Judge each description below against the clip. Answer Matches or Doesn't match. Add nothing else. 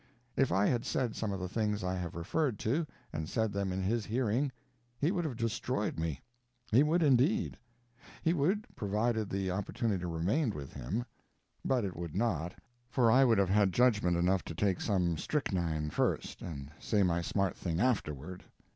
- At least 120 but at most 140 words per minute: Doesn't match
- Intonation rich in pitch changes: Matches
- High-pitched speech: Doesn't match